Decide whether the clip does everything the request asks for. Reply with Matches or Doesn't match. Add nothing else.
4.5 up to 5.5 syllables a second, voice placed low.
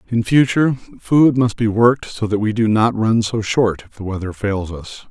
Matches